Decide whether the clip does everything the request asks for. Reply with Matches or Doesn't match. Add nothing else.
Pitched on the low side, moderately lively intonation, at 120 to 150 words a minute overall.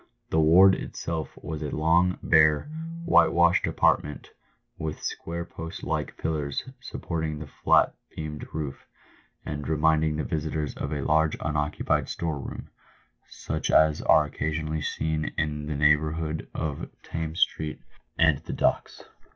Doesn't match